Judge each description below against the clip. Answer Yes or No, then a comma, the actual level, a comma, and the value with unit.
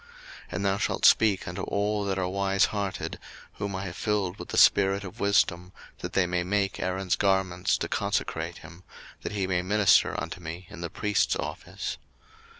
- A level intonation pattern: Yes, narrow, 1.9 semitones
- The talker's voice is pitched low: Yes, very low, 95 Hz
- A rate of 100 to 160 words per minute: No, average, 185 wpm